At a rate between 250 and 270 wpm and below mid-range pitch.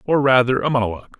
No: average, 200 wpm; low, 125 Hz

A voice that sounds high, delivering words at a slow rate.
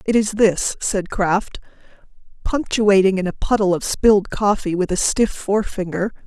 No: high, 200 Hz; average, 155 wpm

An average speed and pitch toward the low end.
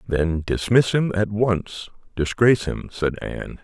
Yes: average, 150 wpm; low, 100 Hz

